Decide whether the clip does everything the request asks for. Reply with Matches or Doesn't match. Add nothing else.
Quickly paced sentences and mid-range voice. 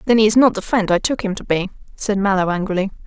Doesn't match